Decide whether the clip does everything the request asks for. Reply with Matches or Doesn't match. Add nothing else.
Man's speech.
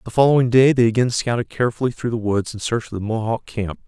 Matches